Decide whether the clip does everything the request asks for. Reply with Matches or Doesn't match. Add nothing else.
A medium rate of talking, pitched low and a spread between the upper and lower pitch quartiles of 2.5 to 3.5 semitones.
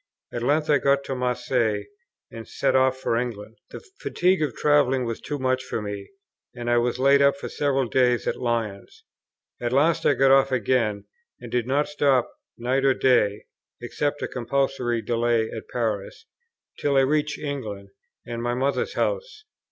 Matches